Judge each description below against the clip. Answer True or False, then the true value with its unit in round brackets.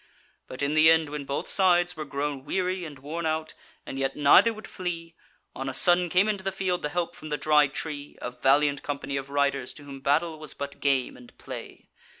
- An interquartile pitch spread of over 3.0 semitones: True (3.6 semitones)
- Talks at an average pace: False (215 wpm)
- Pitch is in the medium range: True (150 Hz)